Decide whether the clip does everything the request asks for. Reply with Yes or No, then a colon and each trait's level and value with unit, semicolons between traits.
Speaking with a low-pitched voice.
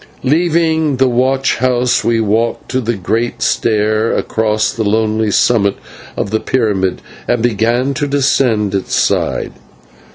Yes: low, 115 Hz